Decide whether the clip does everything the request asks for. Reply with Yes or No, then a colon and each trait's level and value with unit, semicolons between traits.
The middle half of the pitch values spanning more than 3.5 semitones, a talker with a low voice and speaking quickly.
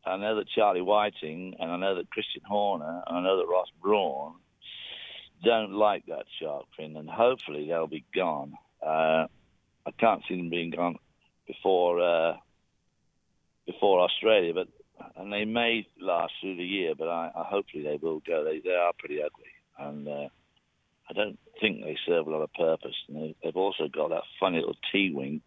No: wide, 5.6 semitones; very low, 90 Hz; average, 185 wpm